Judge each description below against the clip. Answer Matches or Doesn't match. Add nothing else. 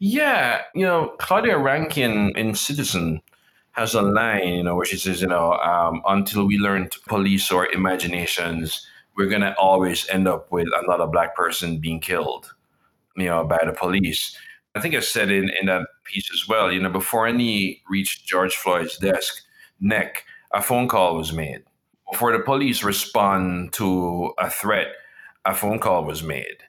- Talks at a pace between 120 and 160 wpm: Doesn't match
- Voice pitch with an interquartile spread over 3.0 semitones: Doesn't match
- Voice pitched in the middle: Doesn't match